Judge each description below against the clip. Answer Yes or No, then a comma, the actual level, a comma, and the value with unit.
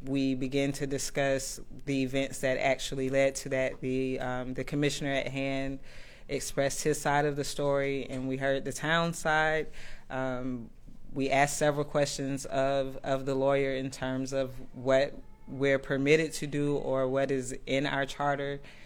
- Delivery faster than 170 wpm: No, average, 165 wpm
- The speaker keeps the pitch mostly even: Yes, narrow, 1.1 semitones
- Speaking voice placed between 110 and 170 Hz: Yes, low, 135 Hz